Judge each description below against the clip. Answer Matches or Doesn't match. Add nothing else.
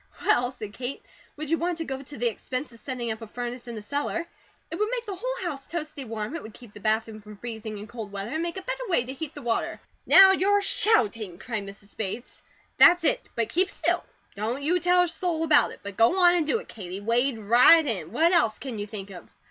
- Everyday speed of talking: Doesn't match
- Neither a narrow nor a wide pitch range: Doesn't match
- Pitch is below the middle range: Doesn't match